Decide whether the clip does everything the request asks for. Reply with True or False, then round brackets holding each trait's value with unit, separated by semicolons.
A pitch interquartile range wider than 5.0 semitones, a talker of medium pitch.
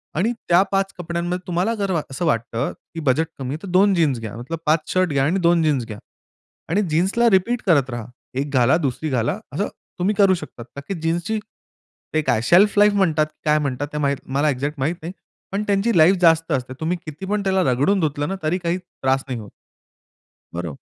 True (5.5 semitones; 165 Hz)